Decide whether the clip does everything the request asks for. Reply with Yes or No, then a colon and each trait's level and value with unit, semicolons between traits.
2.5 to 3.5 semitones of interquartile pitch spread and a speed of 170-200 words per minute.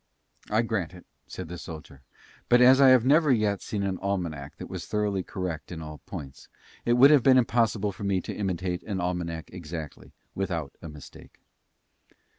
No: average, 5.3 semitones; average, 180 wpm